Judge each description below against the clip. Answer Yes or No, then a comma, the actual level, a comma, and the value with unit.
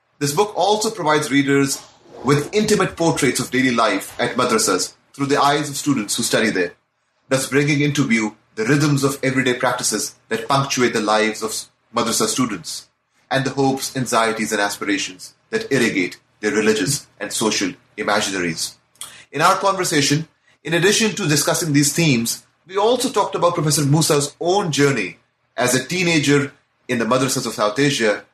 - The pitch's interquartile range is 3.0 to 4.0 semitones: Yes, average, 3.7 semitones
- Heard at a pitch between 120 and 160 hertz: Yes, medium, 140 Hz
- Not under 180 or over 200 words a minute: No, average, 160 wpm